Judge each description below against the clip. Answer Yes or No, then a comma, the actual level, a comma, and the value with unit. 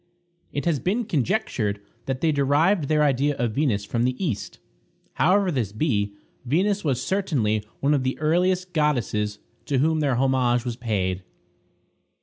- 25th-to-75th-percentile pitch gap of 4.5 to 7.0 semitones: Yes, average, 5.2 semitones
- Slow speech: No, average, 150 wpm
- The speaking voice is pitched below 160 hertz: Yes, medium, 140 Hz